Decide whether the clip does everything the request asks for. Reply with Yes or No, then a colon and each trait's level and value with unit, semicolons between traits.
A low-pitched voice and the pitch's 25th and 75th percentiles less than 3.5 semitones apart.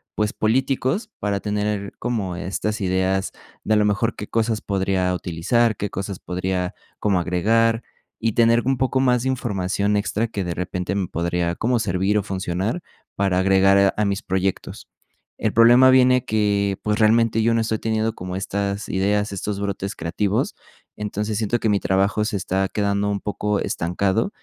Yes: low, 100 Hz; average, 2.8 semitones